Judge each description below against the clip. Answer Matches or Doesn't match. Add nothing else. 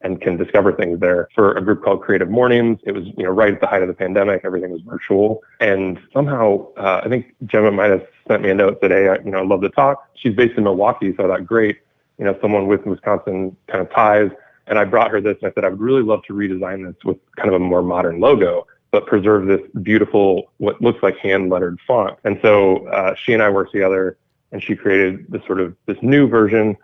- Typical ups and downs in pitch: Matches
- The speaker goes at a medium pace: Doesn't match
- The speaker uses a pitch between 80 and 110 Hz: Matches